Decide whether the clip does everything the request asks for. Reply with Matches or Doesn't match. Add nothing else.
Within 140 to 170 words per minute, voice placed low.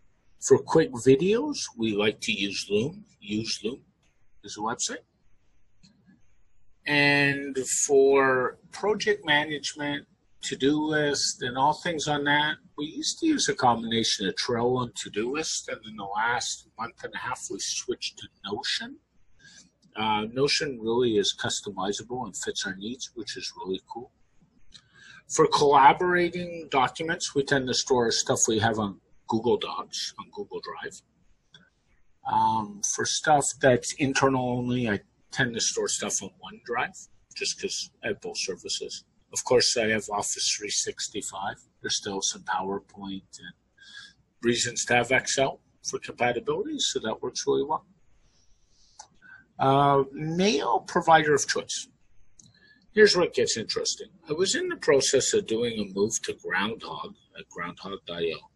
Doesn't match